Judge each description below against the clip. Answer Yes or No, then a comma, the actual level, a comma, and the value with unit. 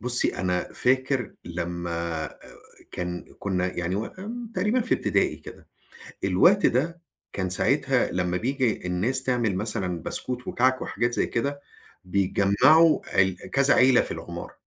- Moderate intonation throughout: No, wide, 6.4 semitones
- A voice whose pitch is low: Yes, low, 105 Hz